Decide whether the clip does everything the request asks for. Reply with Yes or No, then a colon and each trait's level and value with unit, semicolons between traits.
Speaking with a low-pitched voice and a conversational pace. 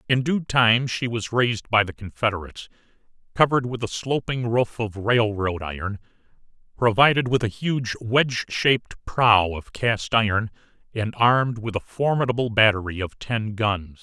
Yes: low, 115 Hz; average, 155 wpm